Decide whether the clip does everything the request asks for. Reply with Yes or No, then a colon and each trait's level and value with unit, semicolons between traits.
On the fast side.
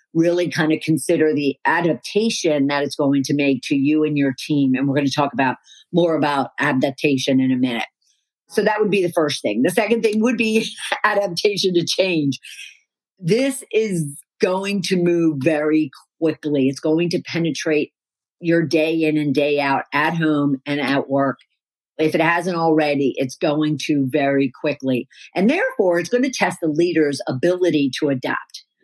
No: average, 175 wpm